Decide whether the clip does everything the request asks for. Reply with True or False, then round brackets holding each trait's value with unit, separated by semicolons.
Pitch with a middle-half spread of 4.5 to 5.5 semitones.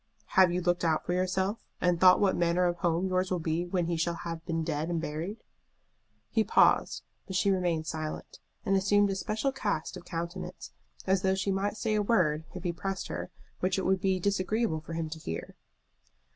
False (2.5 semitones)